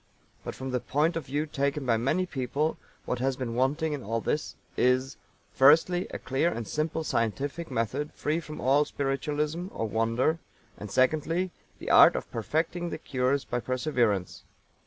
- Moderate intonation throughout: Yes, average, 3.7 semitones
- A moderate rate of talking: Yes, average, 160 wpm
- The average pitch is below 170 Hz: Yes, medium, 140 Hz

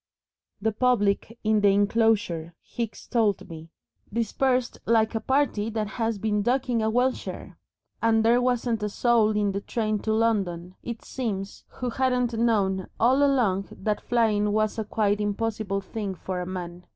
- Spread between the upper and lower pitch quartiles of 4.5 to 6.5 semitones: No, average, 2.7 semitones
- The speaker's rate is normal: Yes, average, 155 wpm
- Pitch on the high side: Yes, high, 220 Hz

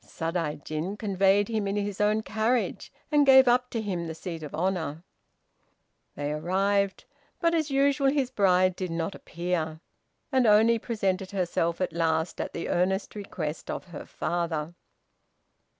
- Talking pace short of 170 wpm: Yes, average, 150 wpm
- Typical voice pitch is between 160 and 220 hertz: Yes, high, 190 Hz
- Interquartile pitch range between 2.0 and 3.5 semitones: No, average, 4.6 semitones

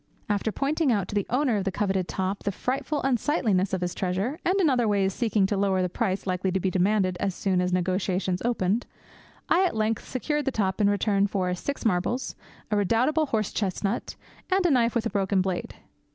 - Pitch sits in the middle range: No, high, 205 Hz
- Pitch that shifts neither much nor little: Yes, average, 4.4 semitones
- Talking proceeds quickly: Yes, fast, 210 wpm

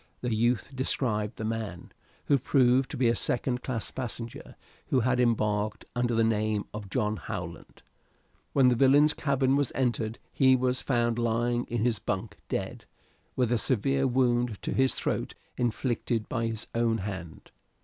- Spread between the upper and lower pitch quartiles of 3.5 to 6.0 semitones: No, average, 2.7 semitones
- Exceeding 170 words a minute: No, average, 160 wpm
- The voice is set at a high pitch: No, low, 120 Hz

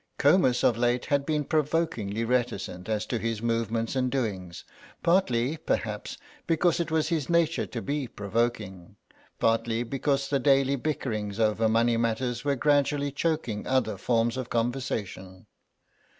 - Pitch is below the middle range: Yes, low, 120 Hz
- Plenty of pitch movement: No, average, 4.1 semitones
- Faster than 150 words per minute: No, average, 140 wpm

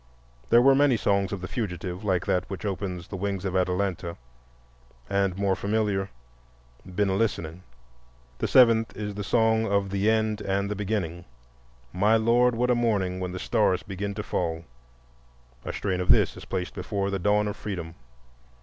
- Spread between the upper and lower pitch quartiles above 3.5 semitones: No, average, 2.8 semitones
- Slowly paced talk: No, average, 175 wpm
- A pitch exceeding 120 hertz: No, low, 100 Hz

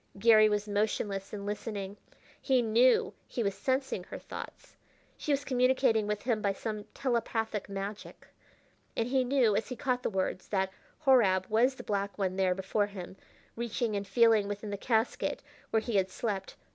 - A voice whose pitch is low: No, high, 215 Hz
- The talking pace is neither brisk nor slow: Yes, average, 170 wpm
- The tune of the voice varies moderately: Yes, average, 3.1 semitones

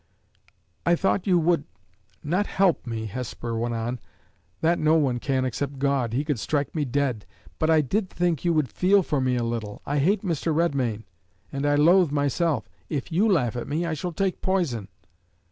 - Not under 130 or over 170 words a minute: No, average, 195 wpm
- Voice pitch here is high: No, medium, 145 Hz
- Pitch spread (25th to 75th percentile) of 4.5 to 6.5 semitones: Yes, wide, 5.4 semitones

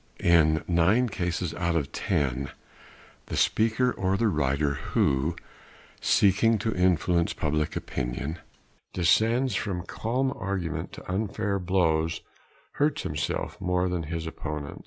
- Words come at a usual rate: No, slow, 120 wpm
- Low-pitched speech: Yes, very low, 90 Hz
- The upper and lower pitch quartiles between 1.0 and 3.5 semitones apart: No, average, 4.6 semitones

